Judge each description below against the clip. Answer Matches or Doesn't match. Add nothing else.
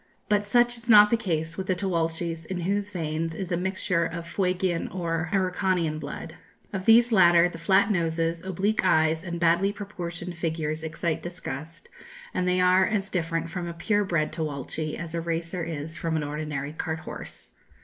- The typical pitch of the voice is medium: Matches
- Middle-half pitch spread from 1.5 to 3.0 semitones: Matches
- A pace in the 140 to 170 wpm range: Doesn't match